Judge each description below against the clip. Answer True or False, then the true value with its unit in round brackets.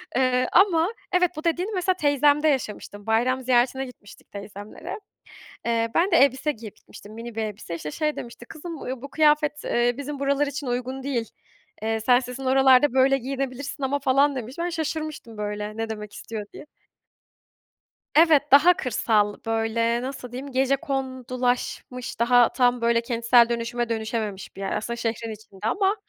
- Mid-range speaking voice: False (255 Hz)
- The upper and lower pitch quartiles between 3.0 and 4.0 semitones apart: True (3.7 semitones)